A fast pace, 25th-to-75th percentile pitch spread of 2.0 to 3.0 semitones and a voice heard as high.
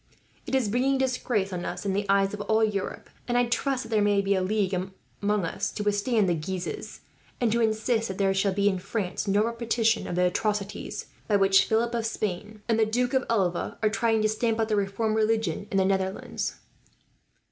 Yes: fast, 215 wpm; narrow, 2.5 semitones; high, 210 Hz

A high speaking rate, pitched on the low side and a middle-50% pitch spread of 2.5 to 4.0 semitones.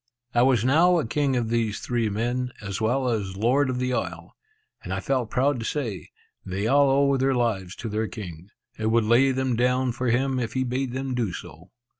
Yes: fast, 215 wpm; low, 120 Hz; average, 3.2 semitones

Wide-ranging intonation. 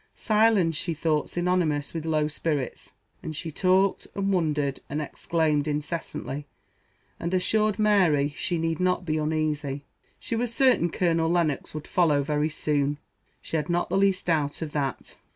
No: average, 3.5 semitones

